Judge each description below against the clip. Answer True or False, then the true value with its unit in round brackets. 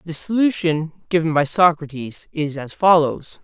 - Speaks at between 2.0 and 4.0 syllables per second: False (4.5 syllables/s)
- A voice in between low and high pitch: True (160 Hz)